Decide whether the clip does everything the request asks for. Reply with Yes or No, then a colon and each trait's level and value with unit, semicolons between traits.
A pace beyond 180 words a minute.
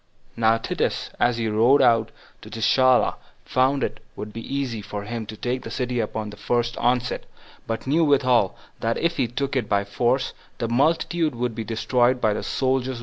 Yes: fast, 205 wpm